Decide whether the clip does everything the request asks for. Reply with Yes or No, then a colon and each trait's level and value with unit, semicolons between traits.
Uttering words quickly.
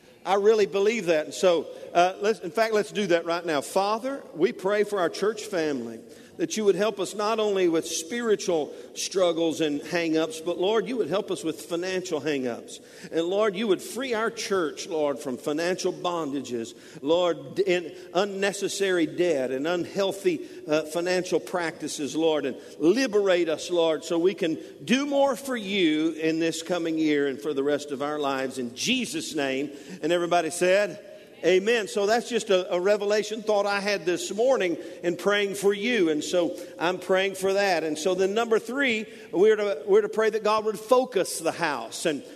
No: average, 185 wpm